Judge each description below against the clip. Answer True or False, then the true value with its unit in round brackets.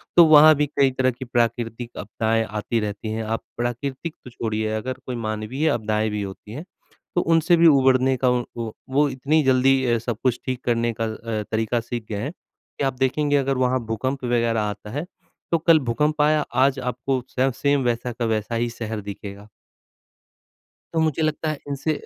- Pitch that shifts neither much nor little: True (3.7 semitones)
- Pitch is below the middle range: True (125 Hz)